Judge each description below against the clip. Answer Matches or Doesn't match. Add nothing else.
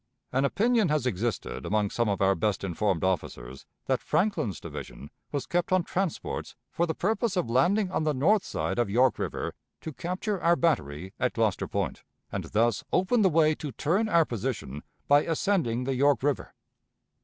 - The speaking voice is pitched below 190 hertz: Matches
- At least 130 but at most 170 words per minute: Doesn't match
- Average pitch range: Doesn't match